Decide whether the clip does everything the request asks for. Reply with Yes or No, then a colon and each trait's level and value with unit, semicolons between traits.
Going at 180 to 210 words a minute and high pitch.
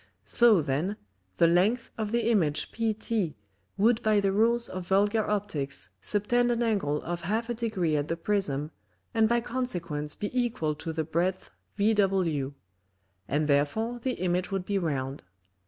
No: average, 155 wpm; high, 195 Hz